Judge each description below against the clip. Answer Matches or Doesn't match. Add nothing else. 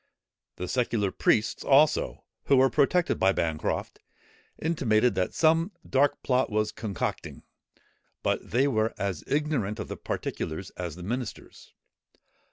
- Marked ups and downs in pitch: Matches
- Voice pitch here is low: Matches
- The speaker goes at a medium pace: Doesn't match